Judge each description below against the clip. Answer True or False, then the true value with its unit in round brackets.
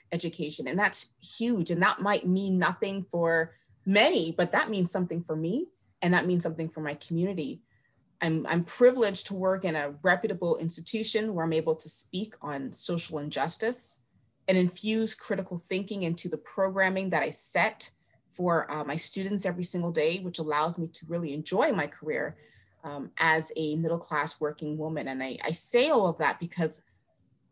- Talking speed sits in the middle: True (175 wpm)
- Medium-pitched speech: True (170 Hz)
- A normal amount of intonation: True (3.2 semitones)